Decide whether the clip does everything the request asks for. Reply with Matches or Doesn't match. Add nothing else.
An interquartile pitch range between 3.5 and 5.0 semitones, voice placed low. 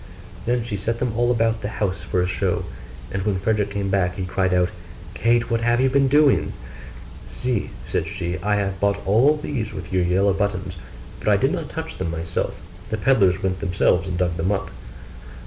Matches